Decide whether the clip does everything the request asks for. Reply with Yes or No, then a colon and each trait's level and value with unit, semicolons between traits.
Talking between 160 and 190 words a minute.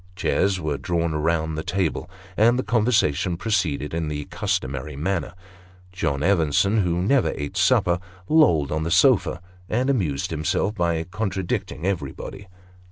No: average, 140 wpm